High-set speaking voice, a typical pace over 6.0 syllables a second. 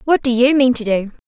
No: high, 245 Hz; 5.7 syllables/s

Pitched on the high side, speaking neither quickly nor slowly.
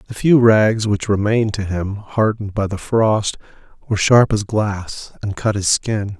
No: low, 105 Hz; average, 185 wpm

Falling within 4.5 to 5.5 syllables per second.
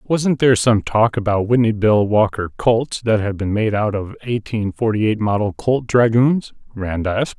Yes: 4.8 syllables/s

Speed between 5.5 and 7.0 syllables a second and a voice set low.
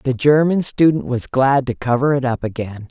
No: 5.0 syllables/s; low, 130 Hz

